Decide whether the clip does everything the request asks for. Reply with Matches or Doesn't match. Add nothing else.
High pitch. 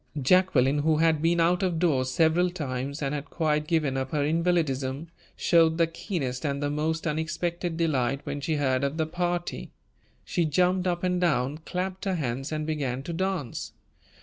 Doesn't match